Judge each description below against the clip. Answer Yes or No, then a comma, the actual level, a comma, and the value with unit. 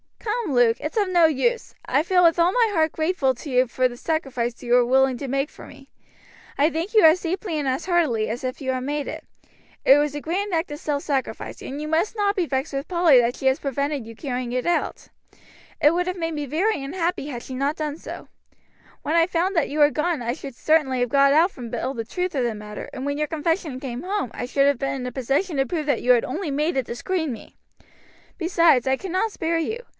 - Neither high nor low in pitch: No, very high, 290 Hz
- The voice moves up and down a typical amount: Yes, average, 4.5 semitones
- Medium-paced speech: No, fast, 250 wpm